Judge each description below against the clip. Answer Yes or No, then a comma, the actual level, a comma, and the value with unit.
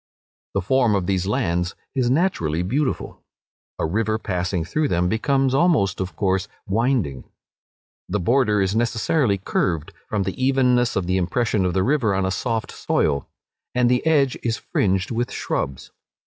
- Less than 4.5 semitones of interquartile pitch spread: No, average, 5.3 semitones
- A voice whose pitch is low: Yes, low, 105 Hz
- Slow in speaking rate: No, average, 160 wpm